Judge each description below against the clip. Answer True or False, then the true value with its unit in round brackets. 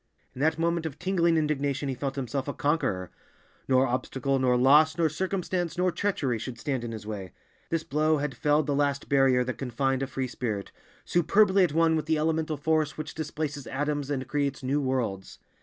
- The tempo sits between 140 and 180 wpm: False (190 wpm)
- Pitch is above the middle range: False (145 Hz)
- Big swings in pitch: False (3.3 semitones)